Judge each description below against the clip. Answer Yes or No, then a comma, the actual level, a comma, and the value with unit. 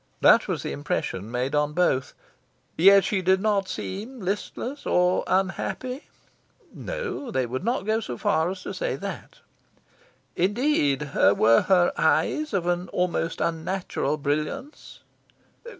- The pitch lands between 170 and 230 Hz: Yes, medium, 185 Hz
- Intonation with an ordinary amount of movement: No, wide, 6.3 semitones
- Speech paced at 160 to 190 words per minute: No, slow, 135 wpm